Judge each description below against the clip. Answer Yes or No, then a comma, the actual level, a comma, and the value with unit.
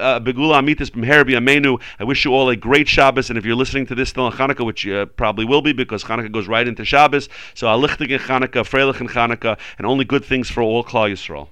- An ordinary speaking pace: No, fast, 225 wpm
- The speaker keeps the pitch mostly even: No, average, 3.2 semitones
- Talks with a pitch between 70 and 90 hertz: No, low, 130 Hz